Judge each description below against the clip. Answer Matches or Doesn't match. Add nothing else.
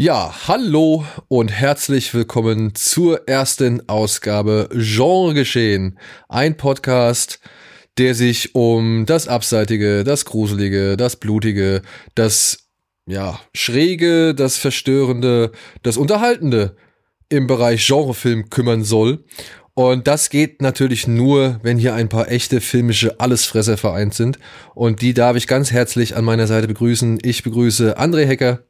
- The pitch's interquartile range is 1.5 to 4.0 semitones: Matches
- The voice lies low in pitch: Matches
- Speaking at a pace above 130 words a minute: Doesn't match